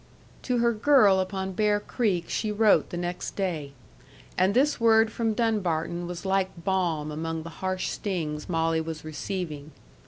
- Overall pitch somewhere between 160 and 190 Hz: Yes, medium, 185 Hz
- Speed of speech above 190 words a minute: No, average, 155 wpm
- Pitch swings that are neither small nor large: Yes, average, 4.5 semitones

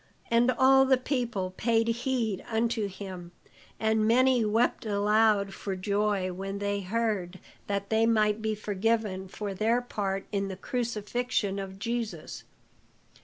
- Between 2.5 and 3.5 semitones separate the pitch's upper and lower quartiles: Yes, average, 2.8 semitones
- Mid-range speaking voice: No, high, 215 Hz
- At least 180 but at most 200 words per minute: No, slow, 135 wpm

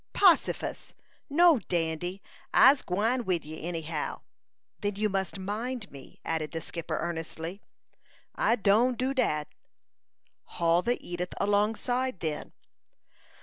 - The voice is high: Yes, high, 195 Hz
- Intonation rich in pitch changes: Yes, wide, 6.3 semitones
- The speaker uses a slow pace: Yes, slow, 120 wpm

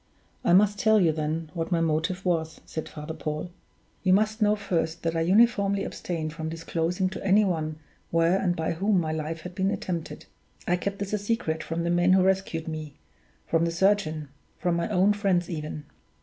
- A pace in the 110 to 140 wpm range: No, average, 195 wpm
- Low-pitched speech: No, medium, 175 Hz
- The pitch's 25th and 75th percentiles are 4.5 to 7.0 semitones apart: No, average, 3.3 semitones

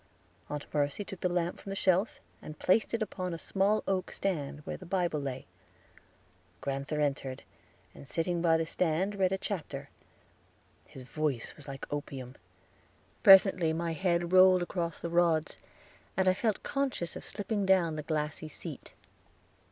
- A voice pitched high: No, medium, 170 Hz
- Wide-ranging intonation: No, average, 4.0 semitones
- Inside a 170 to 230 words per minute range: No, average, 160 wpm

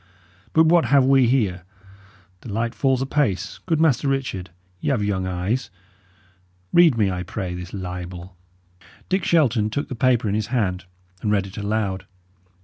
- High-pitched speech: No, low, 110 Hz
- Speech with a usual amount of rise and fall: No, wide, 6.2 semitones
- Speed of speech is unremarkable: Yes, average, 160 wpm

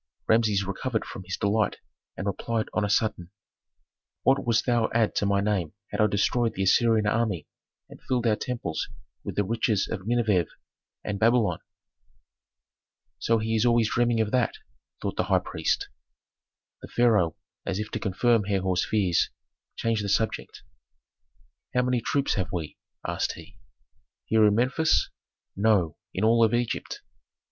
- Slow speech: No, average, 155 wpm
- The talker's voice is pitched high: No, low, 110 Hz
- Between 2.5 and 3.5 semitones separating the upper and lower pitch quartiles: Yes, average, 2.9 semitones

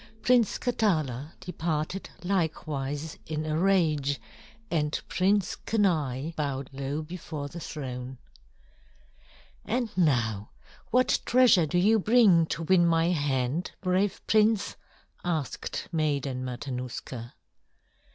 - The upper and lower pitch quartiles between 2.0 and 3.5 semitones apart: No, average, 5.0 semitones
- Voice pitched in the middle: Yes, medium, 160 Hz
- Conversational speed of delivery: No, slow, 105 wpm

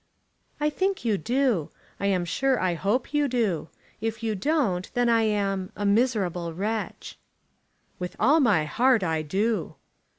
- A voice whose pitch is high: Yes, high, 215 Hz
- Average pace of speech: Yes, average, 155 wpm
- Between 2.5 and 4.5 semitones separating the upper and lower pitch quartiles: No, average, 5.1 semitones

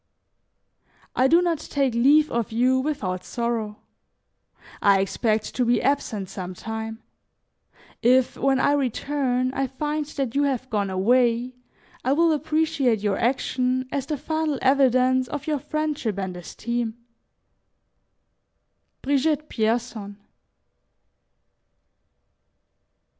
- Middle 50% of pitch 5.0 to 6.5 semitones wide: No, average, 4.2 semitones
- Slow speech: Yes, slow, 110 wpm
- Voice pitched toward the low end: No, very high, 255 Hz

